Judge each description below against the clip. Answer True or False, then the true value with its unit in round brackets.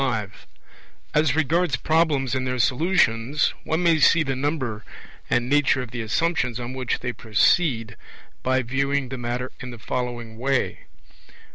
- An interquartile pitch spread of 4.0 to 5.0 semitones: False (3.6 semitones)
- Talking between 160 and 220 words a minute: False (150 wpm)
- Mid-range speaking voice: False (130 Hz)